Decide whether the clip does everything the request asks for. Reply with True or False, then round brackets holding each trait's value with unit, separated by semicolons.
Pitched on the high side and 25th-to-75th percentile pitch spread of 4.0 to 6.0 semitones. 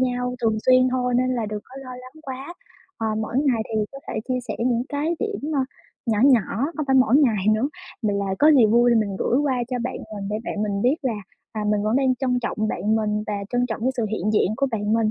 False (245 Hz; 3.3 semitones)